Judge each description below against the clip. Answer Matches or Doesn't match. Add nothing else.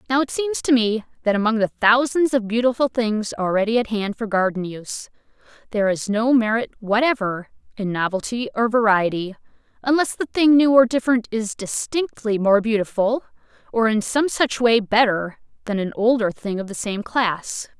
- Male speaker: Doesn't match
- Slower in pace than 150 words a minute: Doesn't match